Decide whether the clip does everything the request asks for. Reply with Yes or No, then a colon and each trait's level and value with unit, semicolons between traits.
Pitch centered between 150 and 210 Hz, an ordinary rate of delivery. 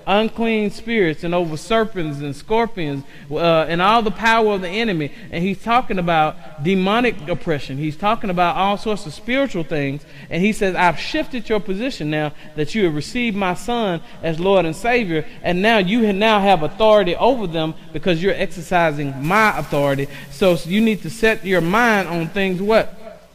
Yes: medium, 185 Hz; average, 185 wpm